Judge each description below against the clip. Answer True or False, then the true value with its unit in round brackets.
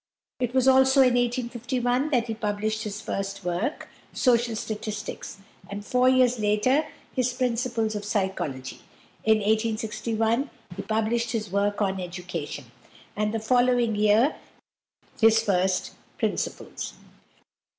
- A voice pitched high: True (220 Hz)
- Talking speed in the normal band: False (120 wpm)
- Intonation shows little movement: False (3.1 semitones)